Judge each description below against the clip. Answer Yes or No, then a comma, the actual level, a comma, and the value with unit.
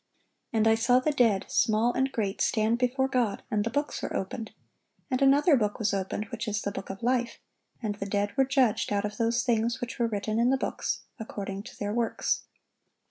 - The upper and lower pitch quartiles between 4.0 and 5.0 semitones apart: No, average, 3.2 semitones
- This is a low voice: No, high, 225 Hz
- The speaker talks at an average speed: No, fast, 210 wpm